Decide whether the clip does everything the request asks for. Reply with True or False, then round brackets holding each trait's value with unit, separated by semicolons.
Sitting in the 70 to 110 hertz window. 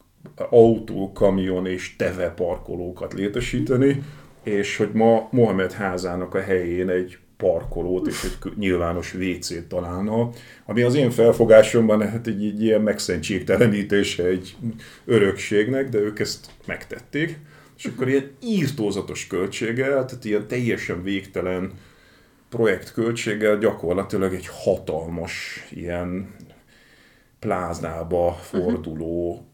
True (100 Hz)